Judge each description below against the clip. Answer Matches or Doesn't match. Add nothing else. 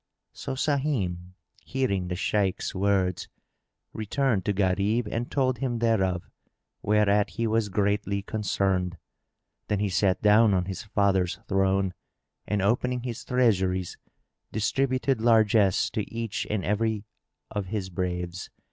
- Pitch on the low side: Matches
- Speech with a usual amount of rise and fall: Matches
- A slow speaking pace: Matches